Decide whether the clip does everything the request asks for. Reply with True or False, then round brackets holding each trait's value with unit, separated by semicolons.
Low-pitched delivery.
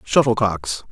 True (130 Hz)